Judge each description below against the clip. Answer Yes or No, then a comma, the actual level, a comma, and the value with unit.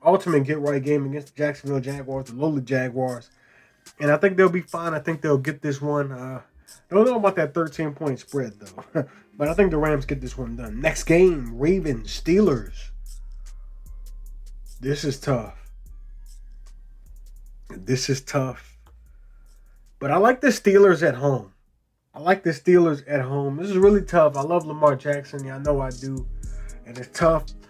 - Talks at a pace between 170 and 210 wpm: Yes, average, 175 wpm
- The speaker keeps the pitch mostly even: No, average, 3.9 semitones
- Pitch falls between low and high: Yes, medium, 145 Hz